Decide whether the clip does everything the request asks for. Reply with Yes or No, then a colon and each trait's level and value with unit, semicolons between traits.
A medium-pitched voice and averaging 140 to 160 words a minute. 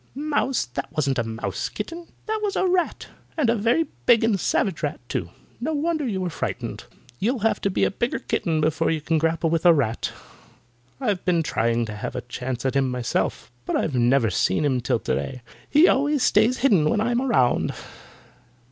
No: medium, 175 Hz; average, 200 wpm